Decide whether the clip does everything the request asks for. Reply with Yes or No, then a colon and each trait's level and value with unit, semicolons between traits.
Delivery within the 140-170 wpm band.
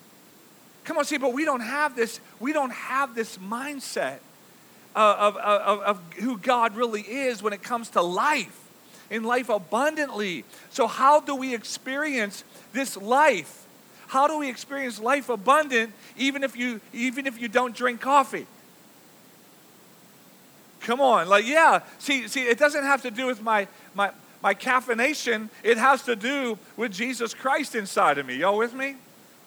Yes: average, 165 wpm